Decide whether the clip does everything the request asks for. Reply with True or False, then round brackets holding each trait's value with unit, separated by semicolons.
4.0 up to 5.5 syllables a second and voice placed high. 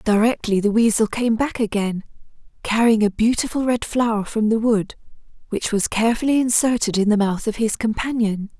True (5.3 syllables/s; 220 Hz)